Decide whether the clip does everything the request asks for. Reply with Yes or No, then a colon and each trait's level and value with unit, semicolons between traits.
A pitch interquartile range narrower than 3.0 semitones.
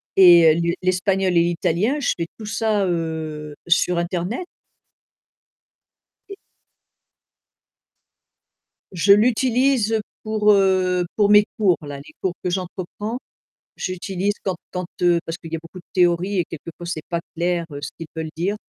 No: average, 3.3 semitones